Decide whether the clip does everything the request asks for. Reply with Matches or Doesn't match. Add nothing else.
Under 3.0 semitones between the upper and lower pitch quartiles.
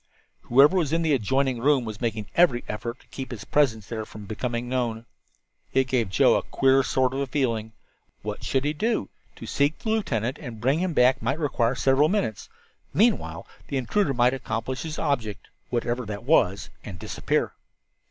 Doesn't match